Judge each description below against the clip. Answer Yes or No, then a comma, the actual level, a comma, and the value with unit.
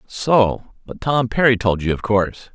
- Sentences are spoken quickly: No, average, 165 wpm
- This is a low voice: Yes, low, 115 Hz